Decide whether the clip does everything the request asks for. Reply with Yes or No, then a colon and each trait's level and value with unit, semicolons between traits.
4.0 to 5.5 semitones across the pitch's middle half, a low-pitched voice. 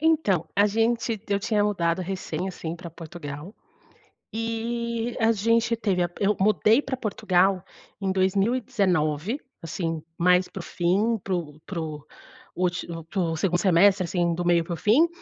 No: average, 4.5 semitones; high, 190 Hz